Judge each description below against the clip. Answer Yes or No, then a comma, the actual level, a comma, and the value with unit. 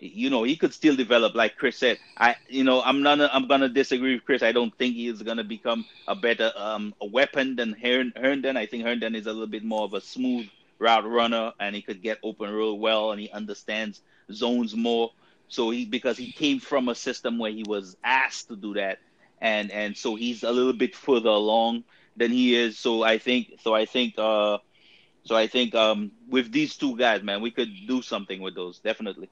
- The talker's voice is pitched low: Yes, low, 115 Hz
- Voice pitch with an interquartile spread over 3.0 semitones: No, average, 2.7 semitones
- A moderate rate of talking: No, fast, 220 wpm